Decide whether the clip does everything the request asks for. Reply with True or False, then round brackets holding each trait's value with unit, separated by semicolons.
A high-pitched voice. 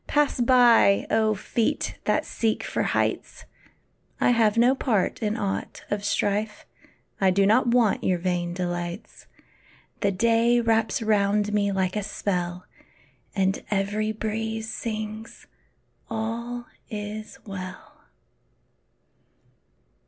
True (215 Hz)